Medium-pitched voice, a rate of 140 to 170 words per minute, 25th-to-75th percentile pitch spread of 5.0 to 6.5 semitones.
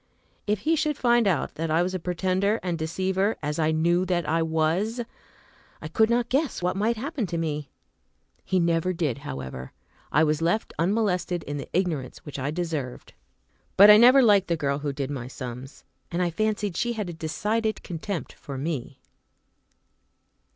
No: medium, 175 Hz; average, 180 wpm; average, 5.3 semitones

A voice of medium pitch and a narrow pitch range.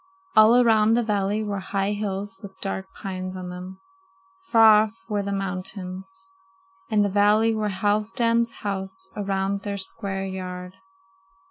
No: high, 200 Hz; narrow, 2.0 semitones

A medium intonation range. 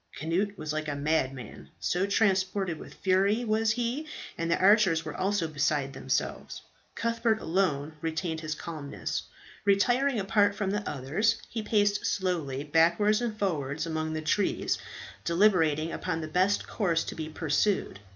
Yes: average, 4.8 semitones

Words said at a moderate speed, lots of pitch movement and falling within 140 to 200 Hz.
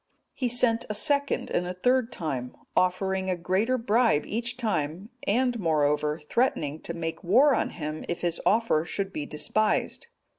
Yes: average, 160 wpm; wide, 6.3 semitones; high, 190 Hz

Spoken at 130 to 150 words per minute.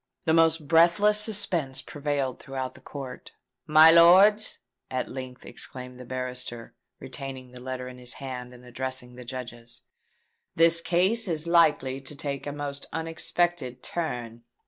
Yes: average, 145 wpm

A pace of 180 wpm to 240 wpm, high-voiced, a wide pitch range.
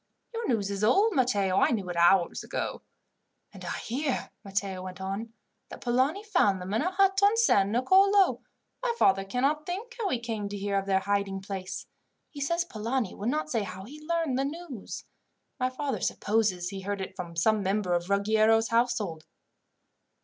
Yes: average, 185 wpm; high, 220 Hz; wide, 6.9 semitones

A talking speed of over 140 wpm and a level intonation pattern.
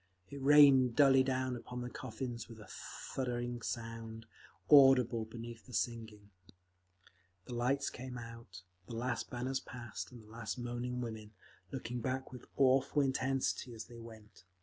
Yes: average, 150 wpm; narrow, 2.2 semitones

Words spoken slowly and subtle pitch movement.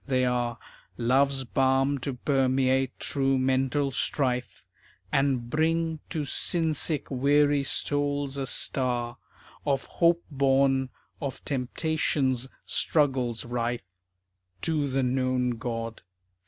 Yes: slow, 105 wpm; narrow, 2.2 semitones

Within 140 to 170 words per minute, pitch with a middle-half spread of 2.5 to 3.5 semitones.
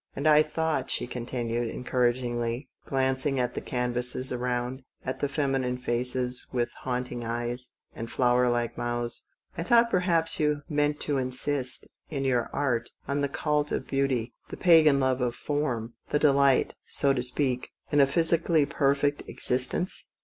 Yes: average, 155 wpm; average, 3.0 semitones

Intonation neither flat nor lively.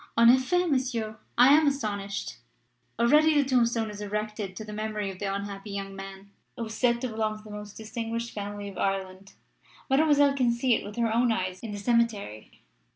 Yes: average, 3.1 semitones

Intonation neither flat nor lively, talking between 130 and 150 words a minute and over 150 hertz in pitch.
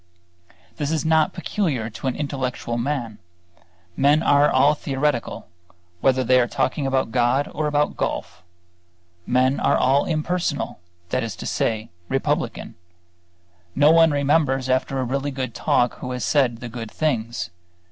No: average, 3.2 semitones; average, 145 wpm; low, 135 Hz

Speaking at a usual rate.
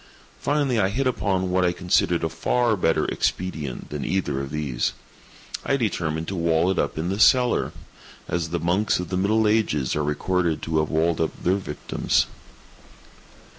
Yes: average, 170 wpm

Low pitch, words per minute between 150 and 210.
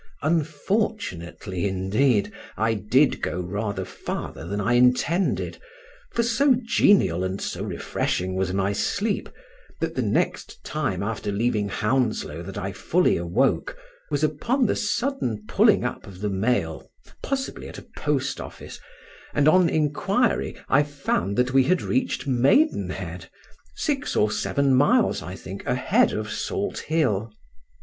No: low, 125 Hz; slow, 135 wpm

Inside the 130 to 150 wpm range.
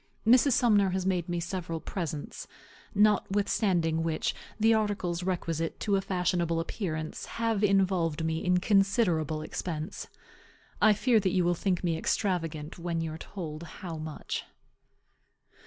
Yes: average, 140 wpm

